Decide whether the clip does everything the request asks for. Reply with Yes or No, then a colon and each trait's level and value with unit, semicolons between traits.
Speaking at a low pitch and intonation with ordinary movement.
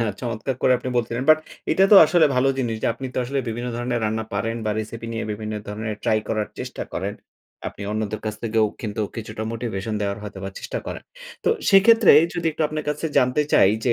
Yes: low, 115 Hz; average, 3.5 semitones